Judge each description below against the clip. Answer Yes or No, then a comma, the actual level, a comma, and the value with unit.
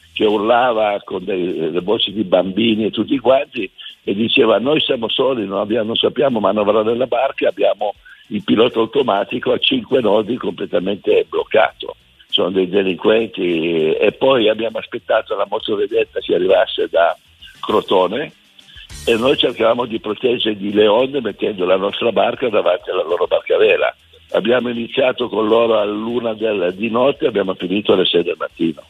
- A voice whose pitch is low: Yes, low, 130 Hz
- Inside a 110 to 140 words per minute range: No, average, 160 wpm